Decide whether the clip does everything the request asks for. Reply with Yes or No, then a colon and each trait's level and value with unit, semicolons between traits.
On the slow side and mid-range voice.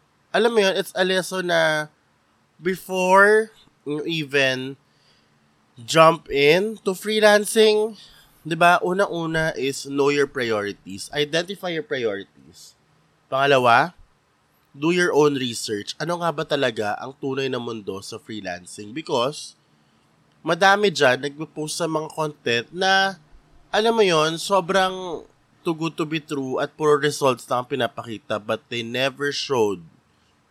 No: average, 130 wpm; medium, 155 Hz